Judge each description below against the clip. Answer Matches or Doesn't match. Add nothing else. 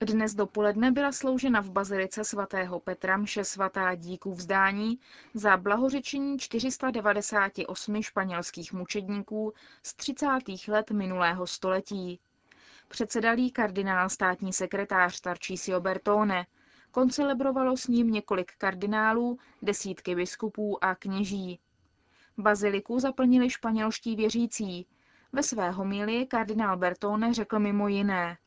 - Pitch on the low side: Doesn't match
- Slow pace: Matches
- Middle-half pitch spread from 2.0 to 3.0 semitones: Doesn't match